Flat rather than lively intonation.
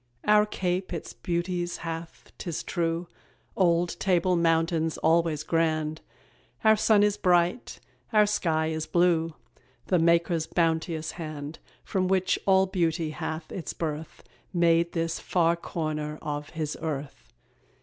Yes: narrow, 2.0 semitones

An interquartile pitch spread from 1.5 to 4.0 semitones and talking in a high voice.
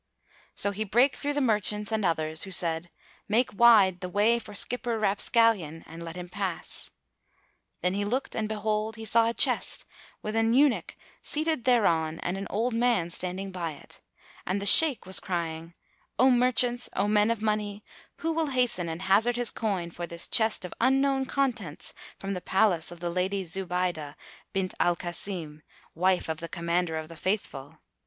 No: average, 4.8 semitones; high, 200 Hz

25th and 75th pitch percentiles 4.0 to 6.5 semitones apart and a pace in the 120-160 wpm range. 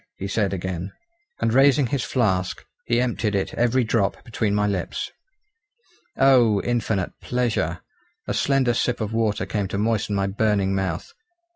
No: average, 3.6 semitones; average, 150 wpm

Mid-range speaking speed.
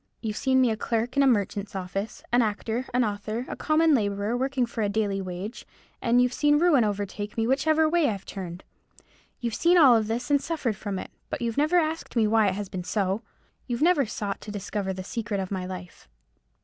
No: fast, 215 wpm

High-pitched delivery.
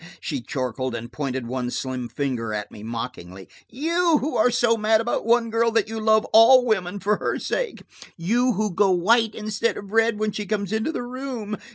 Yes: high, 215 Hz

